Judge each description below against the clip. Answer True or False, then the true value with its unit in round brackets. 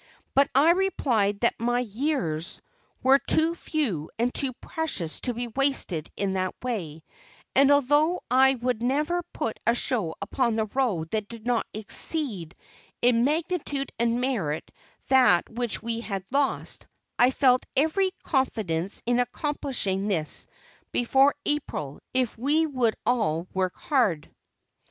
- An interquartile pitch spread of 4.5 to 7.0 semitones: True (5.4 semitones)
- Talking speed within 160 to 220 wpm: False (135 wpm)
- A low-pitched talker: False (245 Hz)